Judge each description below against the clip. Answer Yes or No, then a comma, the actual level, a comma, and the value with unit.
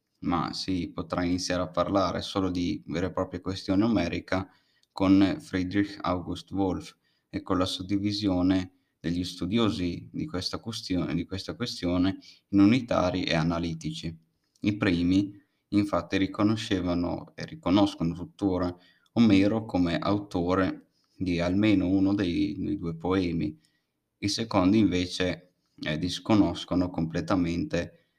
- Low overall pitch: Yes, very low, 90 Hz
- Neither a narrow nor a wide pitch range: No, narrow, 2.0 semitones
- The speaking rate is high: No, average, 120 wpm